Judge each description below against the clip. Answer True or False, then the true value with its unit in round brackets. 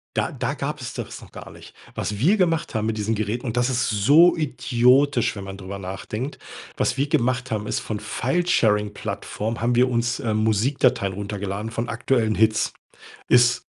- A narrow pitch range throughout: False (3.4 semitones)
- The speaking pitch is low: True (115 Hz)